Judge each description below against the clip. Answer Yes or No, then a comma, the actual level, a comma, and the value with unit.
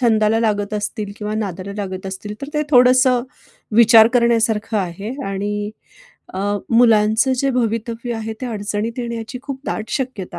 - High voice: Yes, high, 220 Hz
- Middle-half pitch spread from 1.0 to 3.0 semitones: Yes, average, 2.7 semitones